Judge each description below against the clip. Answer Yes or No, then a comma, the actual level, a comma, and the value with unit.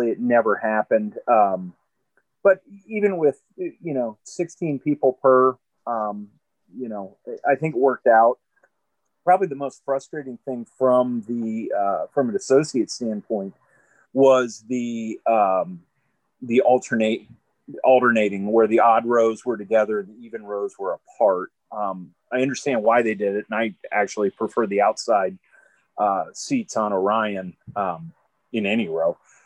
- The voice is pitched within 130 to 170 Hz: No, low, 120 Hz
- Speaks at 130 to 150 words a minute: Yes, average, 145 wpm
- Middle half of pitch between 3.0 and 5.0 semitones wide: Yes, average, 4.2 semitones